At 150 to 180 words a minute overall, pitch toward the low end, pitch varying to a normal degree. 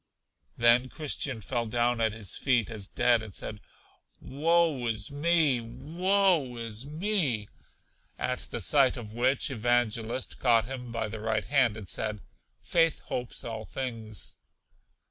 No: average, 140 wpm; low, 120 Hz; average, 3.9 semitones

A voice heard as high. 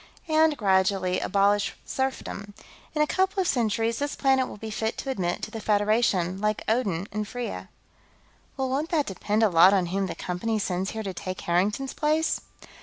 Yes: high, 215 Hz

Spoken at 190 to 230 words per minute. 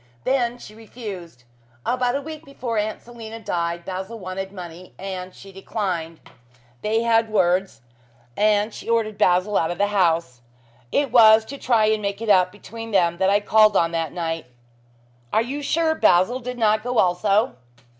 No: average, 170 wpm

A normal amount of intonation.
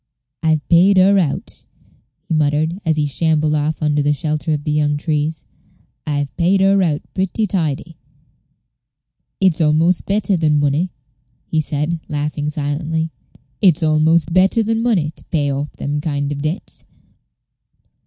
Yes: average, 3.0 semitones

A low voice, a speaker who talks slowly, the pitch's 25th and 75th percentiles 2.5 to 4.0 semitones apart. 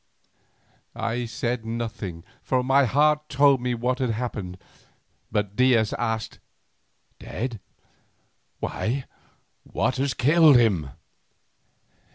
Yes: low, 120 Hz; slow, 95 wpm; average, 2.8 semitones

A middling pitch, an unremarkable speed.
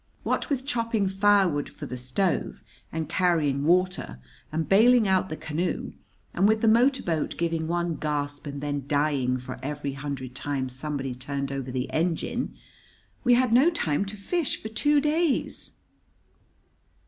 Yes: medium, 160 Hz; average, 155 wpm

